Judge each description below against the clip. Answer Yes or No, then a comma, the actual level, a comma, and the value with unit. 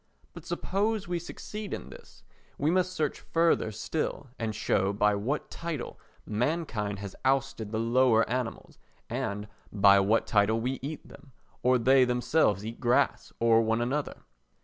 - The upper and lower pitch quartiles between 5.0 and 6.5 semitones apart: Yes, wide, 5.4 semitones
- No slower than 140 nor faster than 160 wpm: Yes, average, 150 wpm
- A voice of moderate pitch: No, low, 125 Hz